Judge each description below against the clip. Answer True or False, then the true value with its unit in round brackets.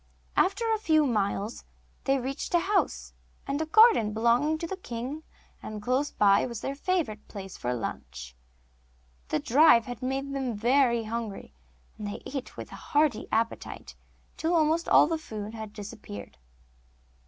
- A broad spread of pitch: True (6.4 semitones)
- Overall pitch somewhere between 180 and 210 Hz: False (250 Hz)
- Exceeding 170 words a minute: False (155 wpm)